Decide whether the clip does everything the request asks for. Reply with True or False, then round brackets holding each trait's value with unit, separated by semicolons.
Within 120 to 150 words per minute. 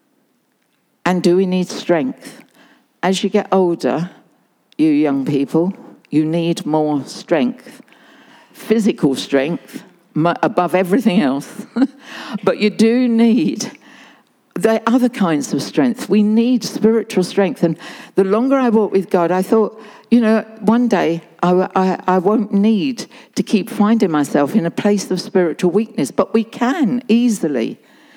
True (140 wpm)